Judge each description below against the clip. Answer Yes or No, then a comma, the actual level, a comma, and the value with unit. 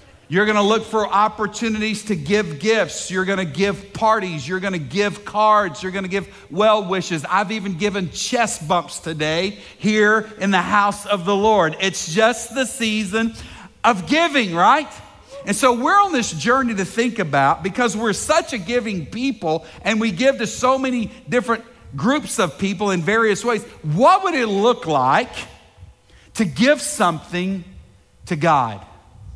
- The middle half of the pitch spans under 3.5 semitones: No, average, 4.4 semitones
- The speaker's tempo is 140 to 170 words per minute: Yes, average, 160 wpm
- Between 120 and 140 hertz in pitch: No, high, 205 Hz